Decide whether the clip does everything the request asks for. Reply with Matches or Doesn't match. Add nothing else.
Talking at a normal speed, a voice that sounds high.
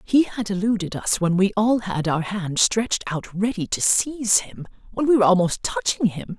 Matches